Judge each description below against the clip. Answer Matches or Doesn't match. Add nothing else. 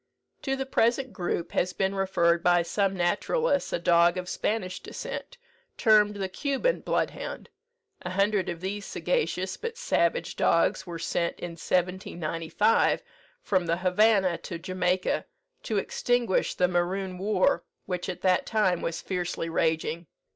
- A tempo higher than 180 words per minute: Doesn't match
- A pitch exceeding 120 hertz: Matches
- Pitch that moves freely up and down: Doesn't match